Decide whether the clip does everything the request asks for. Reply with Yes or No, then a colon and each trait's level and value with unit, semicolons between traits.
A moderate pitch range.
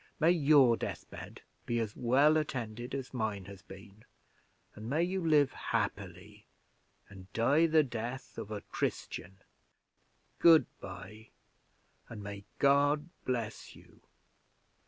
No: wide, 5.7 semitones